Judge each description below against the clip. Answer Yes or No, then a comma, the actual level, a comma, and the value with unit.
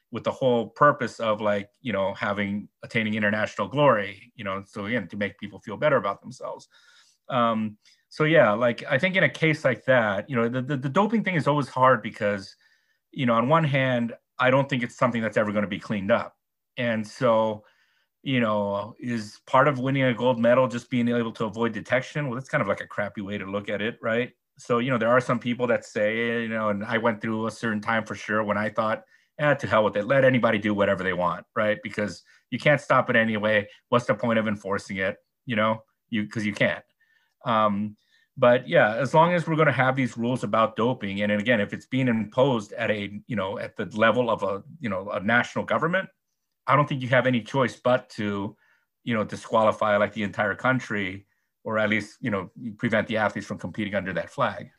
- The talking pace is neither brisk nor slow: No, fast, 230 wpm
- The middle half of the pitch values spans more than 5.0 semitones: No, average, 3.7 semitones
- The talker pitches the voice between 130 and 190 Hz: No, low, 115 Hz